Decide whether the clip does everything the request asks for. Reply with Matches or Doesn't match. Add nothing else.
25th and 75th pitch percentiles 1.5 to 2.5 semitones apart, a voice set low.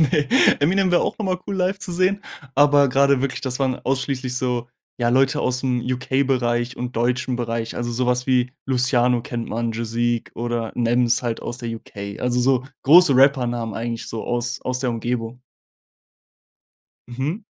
Matches